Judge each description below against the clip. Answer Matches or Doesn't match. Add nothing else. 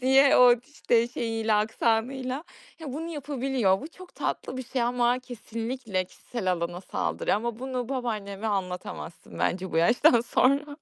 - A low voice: Doesn't match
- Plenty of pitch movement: Doesn't match